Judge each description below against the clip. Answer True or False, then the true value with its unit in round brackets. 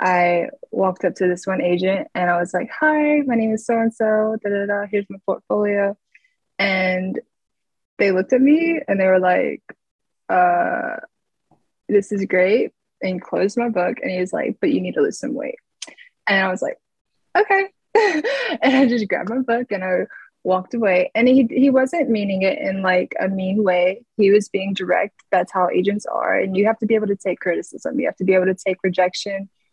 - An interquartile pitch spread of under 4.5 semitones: False (5.4 semitones)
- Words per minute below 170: False (205 wpm)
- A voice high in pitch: True (200 Hz)